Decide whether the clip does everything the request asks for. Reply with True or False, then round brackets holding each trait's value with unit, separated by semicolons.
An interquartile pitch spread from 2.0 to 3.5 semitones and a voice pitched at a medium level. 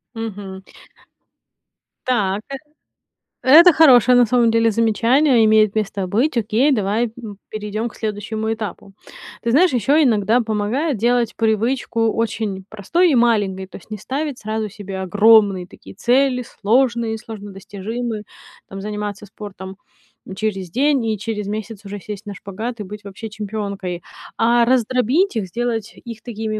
False (2.8 semitones; 220 Hz)